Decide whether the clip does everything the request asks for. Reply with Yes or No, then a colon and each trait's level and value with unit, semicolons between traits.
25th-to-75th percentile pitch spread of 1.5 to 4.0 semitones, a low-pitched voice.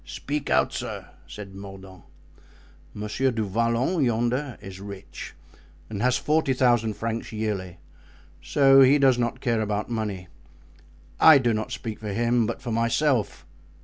Yes: average, 3.6 semitones; low, 115 Hz